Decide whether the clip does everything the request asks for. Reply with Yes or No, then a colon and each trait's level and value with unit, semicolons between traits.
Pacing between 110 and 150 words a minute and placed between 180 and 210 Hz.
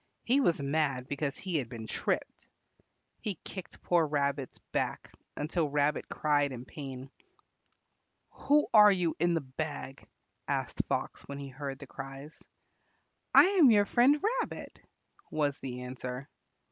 No: average, 140 wpm; medium, 145 Hz